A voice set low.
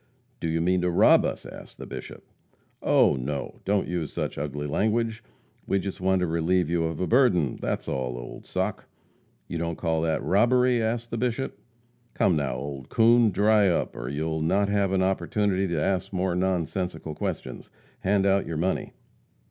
Yes: very low, 90 Hz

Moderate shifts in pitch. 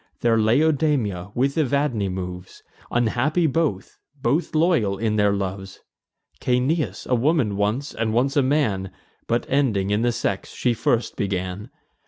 No: wide, 5.9 semitones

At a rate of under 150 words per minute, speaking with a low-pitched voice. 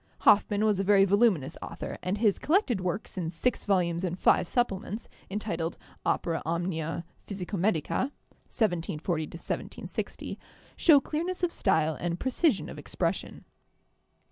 No: average, 140 wpm; high, 190 Hz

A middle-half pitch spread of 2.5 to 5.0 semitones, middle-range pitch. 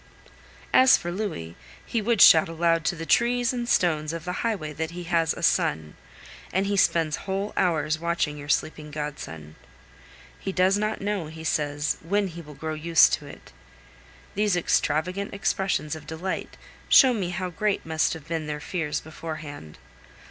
Yes: average, 4.0 semitones; medium, 165 Hz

